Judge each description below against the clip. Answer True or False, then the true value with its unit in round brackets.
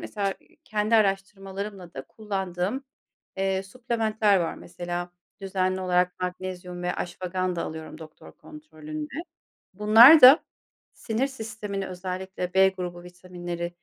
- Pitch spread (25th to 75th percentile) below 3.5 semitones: True (2.8 semitones)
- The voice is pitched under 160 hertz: False (190 Hz)